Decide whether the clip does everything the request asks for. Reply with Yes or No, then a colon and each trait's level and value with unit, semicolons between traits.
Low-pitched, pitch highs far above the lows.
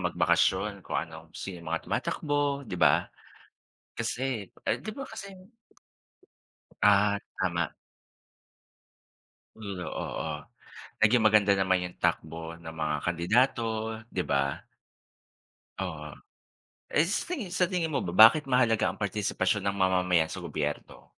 Yes: low, 100 Hz; wide, 6.2 semitones